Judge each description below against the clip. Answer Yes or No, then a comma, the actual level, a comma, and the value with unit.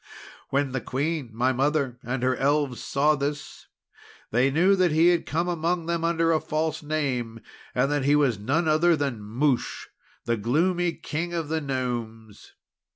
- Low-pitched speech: No, medium, 145 Hz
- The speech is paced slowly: No, average, 165 wpm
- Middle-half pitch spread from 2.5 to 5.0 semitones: Yes, average, 4.2 semitones